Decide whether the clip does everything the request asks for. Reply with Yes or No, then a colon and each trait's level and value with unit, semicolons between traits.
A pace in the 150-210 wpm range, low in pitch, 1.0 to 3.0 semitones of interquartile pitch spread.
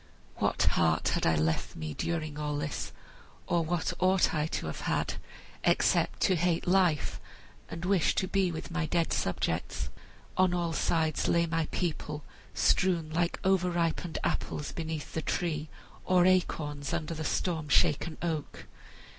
No: average, 155 wpm; medium, 165 Hz; average, 2.7 semitones